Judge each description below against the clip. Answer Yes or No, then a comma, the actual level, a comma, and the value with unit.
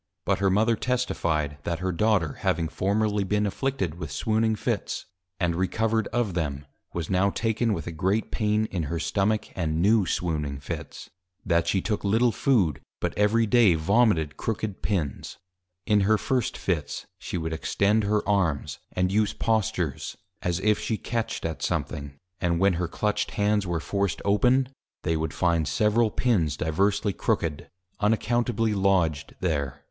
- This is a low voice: Yes, low, 100 Hz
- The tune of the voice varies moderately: Yes, average, 4.7 semitones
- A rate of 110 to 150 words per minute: No, average, 160 wpm